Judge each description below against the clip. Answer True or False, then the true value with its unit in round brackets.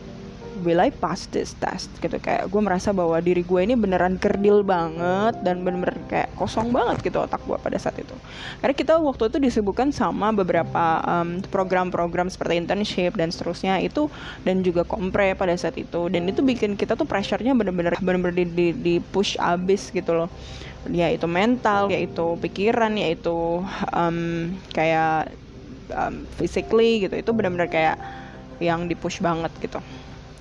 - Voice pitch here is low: False (180 Hz)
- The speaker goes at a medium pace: False (160 wpm)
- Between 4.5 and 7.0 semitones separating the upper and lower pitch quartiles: False (3.2 semitones)